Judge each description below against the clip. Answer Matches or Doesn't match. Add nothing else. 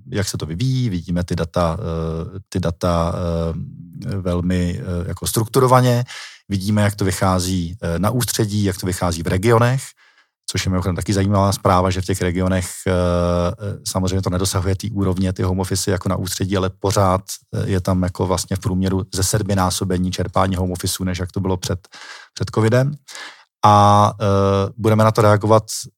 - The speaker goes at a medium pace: Matches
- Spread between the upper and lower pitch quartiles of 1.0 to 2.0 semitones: Doesn't match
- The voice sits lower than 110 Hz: Matches